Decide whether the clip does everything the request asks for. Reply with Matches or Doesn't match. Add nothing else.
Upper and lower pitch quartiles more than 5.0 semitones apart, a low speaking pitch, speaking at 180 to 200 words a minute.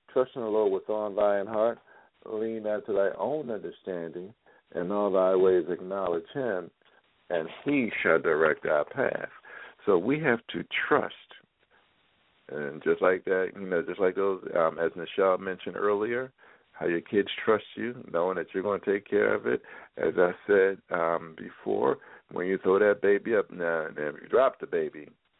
Matches